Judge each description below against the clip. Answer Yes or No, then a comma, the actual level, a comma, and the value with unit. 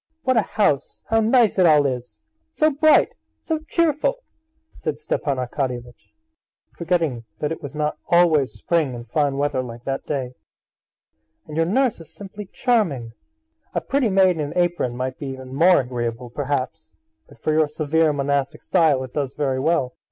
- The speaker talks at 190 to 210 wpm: No, average, 165 wpm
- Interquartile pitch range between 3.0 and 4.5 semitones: No, wide, 5.4 semitones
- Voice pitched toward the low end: No, medium, 150 Hz